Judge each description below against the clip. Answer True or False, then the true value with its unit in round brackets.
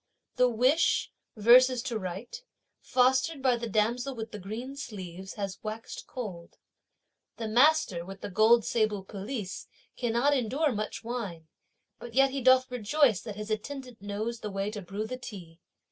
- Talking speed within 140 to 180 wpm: True (160 wpm)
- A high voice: True (225 Hz)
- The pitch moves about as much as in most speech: True (3.8 semitones)